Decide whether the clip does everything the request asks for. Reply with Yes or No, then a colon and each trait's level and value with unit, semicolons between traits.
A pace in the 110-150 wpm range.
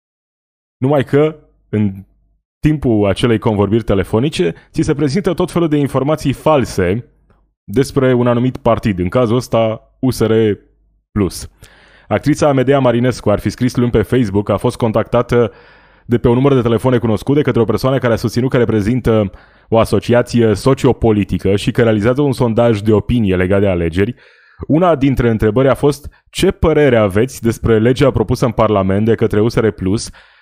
No: average, 160 wpm